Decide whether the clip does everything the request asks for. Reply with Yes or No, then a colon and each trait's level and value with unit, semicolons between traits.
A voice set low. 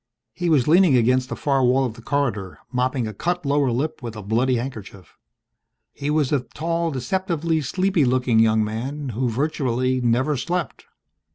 Yes: low, 130 Hz